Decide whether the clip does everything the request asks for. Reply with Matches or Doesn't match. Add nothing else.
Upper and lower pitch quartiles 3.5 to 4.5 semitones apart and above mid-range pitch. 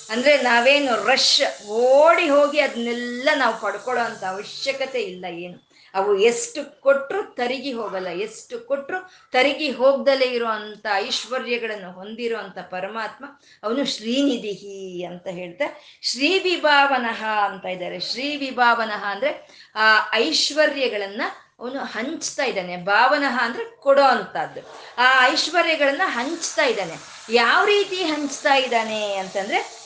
Doesn't match